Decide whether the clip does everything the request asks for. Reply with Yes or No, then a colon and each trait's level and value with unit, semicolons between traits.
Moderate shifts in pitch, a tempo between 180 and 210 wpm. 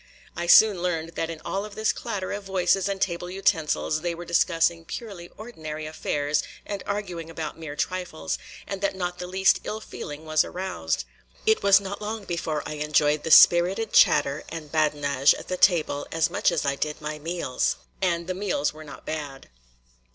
Yes: average, 3.9 semitones; average, 185 wpm